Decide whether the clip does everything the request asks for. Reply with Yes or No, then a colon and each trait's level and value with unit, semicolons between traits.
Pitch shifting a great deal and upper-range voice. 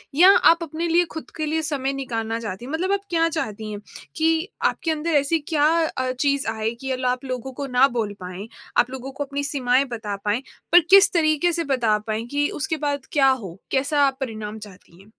Yes: wide, 6.0 semitones; very high, 270 Hz